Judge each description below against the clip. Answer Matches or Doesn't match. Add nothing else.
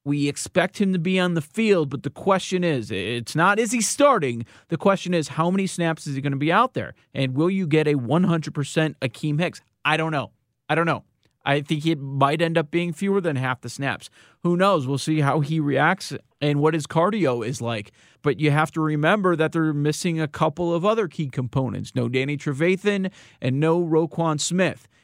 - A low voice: Doesn't match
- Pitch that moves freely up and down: Doesn't match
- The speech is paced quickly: Matches